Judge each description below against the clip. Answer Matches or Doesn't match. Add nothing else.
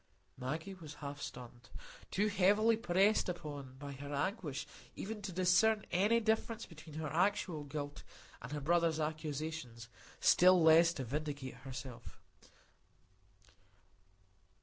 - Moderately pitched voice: Matches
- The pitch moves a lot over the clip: Doesn't match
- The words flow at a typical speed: Doesn't match